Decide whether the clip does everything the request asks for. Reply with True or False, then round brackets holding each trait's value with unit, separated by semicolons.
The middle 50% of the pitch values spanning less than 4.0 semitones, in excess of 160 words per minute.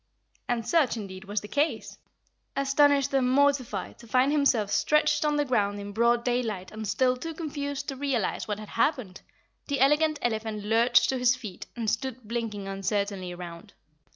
False (5.1 semitones; 170 wpm)